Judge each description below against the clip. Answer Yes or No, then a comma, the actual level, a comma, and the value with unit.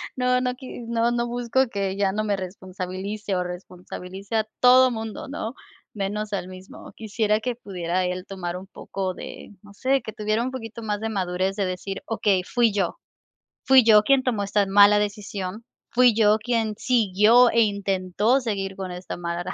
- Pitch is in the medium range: No, high, 210 Hz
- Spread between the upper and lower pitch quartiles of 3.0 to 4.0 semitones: Yes, average, 3.3 semitones